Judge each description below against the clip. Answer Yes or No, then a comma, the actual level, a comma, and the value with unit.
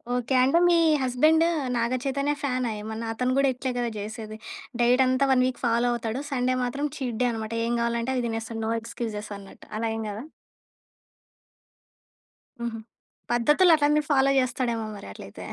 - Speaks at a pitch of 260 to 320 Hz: No, high, 245 Hz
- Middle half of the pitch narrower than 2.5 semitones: No, average, 2.8 semitones